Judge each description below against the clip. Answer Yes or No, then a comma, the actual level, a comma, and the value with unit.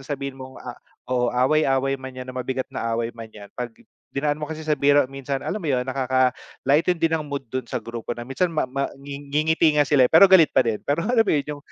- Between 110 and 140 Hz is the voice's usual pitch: Yes, low, 135 Hz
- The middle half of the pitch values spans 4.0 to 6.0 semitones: No, average, 2.8 semitones